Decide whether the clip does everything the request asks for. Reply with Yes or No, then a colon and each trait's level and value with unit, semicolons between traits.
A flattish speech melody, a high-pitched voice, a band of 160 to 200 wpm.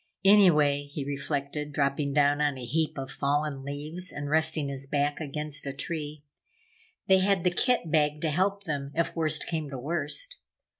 No: narrow, 2.3 semitones; medium, 150 Hz; average, 170 wpm